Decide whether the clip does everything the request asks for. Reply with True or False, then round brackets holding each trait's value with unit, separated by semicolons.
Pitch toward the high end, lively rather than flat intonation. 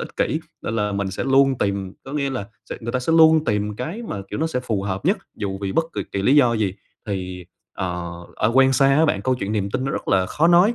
False (115 Hz; 5.8 semitones)